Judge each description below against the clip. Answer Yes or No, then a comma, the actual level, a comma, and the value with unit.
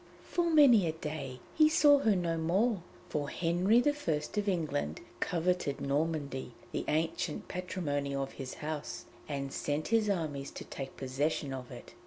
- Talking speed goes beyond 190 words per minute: No, average, 155 wpm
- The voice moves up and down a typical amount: No, wide, 5.8 semitones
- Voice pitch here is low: No, medium, 160 Hz